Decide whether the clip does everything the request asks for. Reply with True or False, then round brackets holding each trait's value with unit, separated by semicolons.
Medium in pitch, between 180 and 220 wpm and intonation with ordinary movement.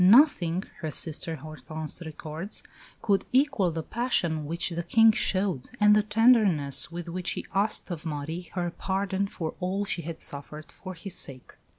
False (175 Hz; 165 wpm; 4.1 semitones)